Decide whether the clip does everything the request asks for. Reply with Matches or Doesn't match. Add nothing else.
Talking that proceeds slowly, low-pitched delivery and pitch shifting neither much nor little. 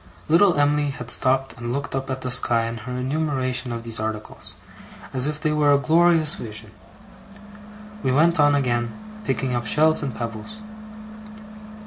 Doesn't match